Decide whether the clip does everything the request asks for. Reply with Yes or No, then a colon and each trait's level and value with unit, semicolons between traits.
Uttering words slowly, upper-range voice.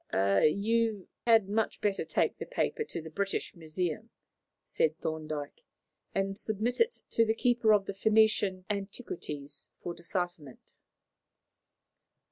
Yes: slow, 120 wpm; high, 195 Hz